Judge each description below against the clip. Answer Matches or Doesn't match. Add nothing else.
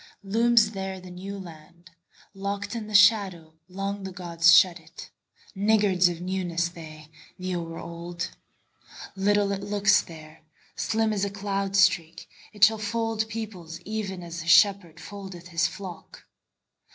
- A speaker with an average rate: Doesn't match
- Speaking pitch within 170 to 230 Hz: Matches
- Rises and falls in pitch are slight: Doesn't match